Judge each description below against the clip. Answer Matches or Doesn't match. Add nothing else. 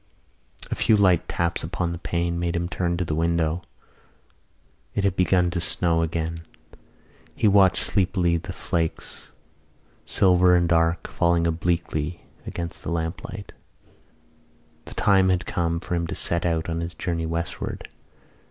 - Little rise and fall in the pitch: Matches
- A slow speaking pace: Doesn't match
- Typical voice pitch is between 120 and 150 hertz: Doesn't match